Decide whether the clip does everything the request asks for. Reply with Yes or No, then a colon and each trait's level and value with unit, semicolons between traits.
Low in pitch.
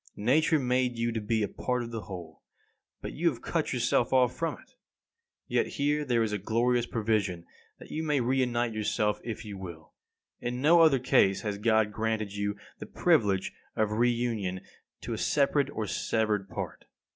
Yes: low, 115 Hz